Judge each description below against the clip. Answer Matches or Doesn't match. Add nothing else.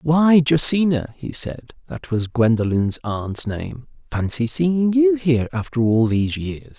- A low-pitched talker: Matches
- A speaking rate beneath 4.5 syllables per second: Matches